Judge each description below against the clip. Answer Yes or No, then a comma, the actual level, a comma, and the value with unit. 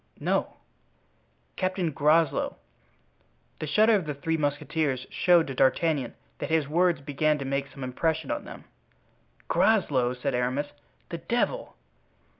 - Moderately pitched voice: Yes, medium, 150 Hz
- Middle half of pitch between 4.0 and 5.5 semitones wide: No, average, 3.1 semitones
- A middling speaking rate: No, slow, 130 wpm